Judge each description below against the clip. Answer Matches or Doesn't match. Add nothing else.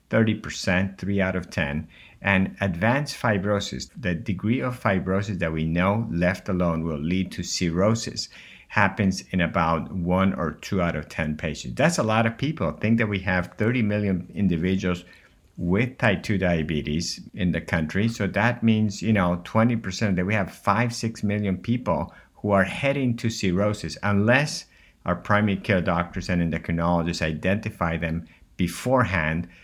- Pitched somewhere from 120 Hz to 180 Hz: Doesn't match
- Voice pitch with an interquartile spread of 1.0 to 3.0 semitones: Doesn't match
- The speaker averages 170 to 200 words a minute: Doesn't match